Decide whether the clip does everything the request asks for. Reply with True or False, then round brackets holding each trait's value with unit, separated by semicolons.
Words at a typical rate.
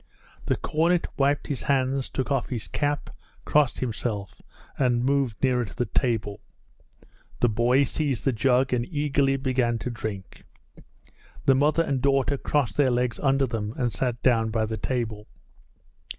True (155 wpm)